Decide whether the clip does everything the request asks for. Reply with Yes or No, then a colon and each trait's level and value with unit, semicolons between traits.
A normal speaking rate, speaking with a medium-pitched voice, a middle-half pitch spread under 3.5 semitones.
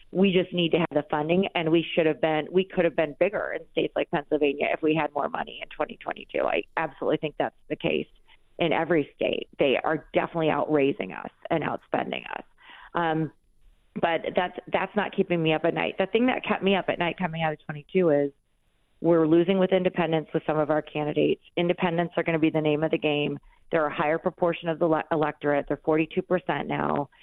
No: fast, 220 wpm; medium, 165 Hz; average, 2.9 semitones